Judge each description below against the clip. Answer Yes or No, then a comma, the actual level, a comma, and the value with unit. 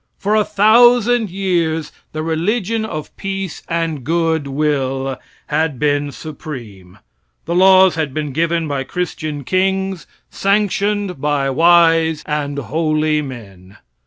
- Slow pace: Yes, slow, 120 wpm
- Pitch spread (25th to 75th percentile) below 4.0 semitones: No, average, 4.7 semitones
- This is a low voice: No, medium, 160 Hz